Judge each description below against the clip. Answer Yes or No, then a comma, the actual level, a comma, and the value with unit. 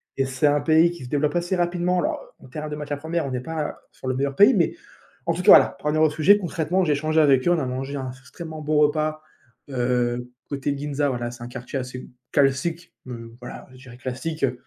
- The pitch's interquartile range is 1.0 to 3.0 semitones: No, average, 3.7 semitones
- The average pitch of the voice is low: No, medium, 145 Hz